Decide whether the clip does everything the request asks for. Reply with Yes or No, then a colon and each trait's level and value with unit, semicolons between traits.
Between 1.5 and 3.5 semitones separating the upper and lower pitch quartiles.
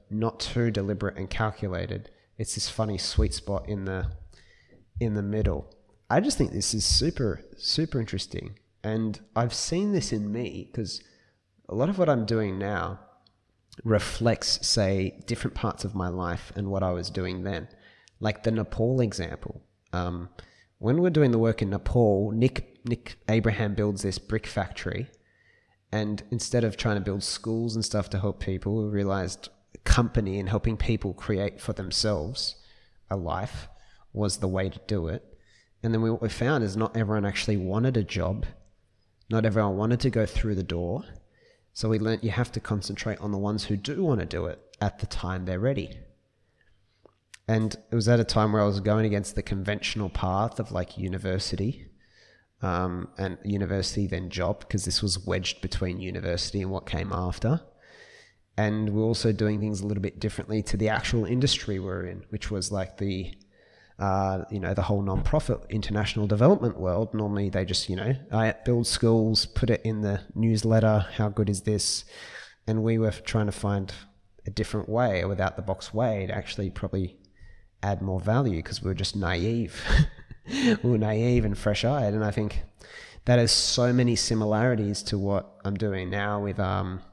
Yes: average, 2.8 semitones